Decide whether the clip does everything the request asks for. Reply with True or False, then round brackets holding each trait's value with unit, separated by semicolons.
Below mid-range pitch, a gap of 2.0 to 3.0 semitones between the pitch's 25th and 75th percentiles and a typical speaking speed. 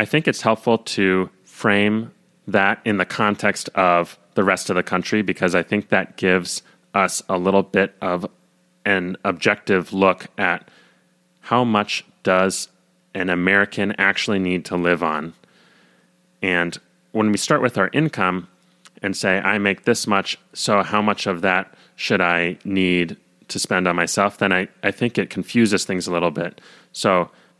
True (95 Hz; 2.4 semitones; 165 wpm)